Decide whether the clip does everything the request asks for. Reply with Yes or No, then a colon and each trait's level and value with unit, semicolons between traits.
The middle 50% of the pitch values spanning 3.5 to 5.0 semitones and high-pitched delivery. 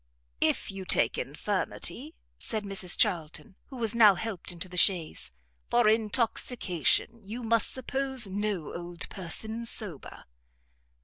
Yes: average, 4.3 semitones; high, 205 Hz